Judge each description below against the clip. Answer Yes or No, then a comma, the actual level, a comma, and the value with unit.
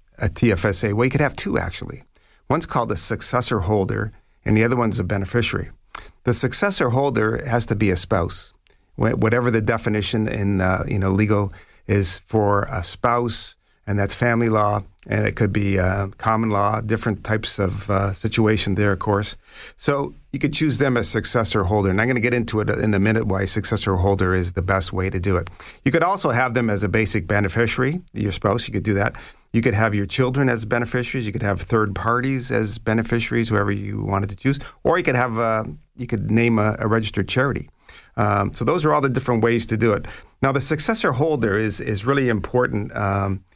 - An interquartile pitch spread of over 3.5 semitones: No, average, 3.1 semitones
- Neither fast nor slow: No, fast, 210 wpm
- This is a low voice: Yes, low, 110 Hz